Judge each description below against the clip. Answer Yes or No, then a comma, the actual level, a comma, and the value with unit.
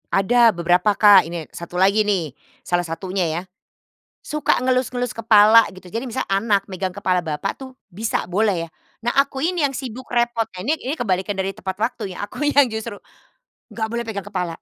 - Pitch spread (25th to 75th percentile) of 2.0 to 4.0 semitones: No, average, 4.5 semitones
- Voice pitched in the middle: No, high, 205 Hz